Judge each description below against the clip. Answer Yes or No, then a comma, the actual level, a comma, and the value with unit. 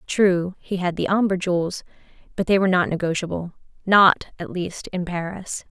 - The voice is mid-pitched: Yes, medium, 180 Hz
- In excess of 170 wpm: No, average, 155 wpm